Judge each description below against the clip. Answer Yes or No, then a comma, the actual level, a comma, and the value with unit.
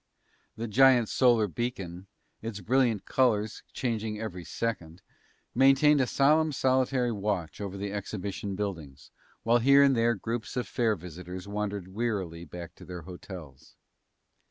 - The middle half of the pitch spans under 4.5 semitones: No, average, 4.9 semitones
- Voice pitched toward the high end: No, low, 105 Hz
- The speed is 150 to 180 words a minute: No, slow, 135 wpm